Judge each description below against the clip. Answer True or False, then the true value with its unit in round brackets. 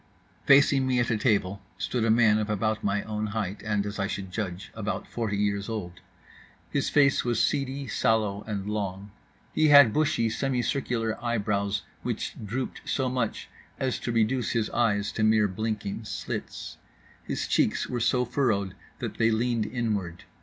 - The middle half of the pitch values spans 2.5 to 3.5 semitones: True (3.0 semitones)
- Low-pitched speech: True (110 Hz)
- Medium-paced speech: True (165 wpm)